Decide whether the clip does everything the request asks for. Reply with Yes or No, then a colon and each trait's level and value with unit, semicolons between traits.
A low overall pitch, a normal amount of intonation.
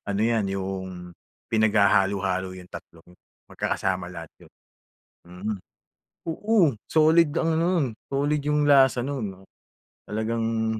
No: low, 110 Hz; wide, 7.0 semitones